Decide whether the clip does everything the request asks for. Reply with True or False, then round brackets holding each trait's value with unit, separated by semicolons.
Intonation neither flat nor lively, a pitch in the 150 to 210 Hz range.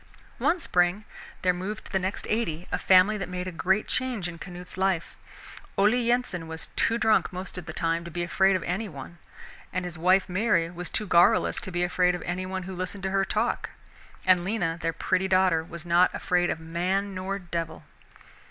False (2.0 semitones; 185 Hz)